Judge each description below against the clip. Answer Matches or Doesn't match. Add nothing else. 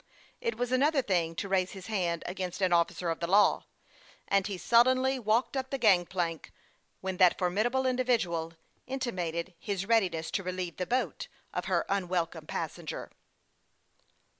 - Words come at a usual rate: Matches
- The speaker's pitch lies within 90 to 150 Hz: Doesn't match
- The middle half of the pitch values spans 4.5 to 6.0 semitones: Matches